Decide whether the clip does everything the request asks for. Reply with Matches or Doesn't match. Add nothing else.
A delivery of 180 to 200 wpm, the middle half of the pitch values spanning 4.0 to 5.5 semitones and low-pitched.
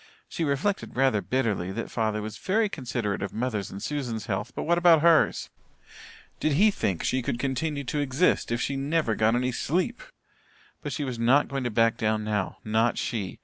Matches